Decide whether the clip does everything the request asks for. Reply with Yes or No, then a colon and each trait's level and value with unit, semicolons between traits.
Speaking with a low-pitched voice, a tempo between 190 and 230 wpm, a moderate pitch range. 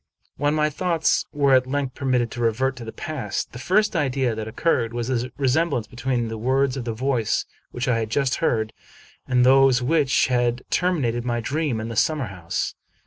Yes: low, 130 Hz; average, 195 wpm; average, 3.1 semitones